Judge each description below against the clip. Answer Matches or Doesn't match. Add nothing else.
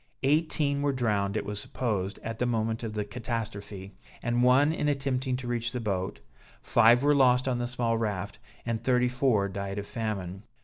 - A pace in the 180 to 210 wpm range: Matches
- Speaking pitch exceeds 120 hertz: Doesn't match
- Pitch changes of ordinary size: Matches